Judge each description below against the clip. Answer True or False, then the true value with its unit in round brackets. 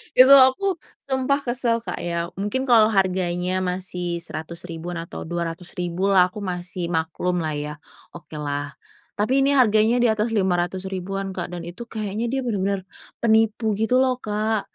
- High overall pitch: True (195 Hz)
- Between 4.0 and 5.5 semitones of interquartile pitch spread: True (4.7 semitones)